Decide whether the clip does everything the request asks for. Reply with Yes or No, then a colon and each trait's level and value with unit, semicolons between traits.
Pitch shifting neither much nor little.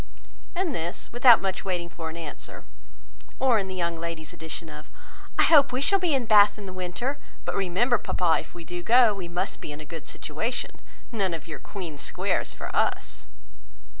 No: wide, 6.0 semitones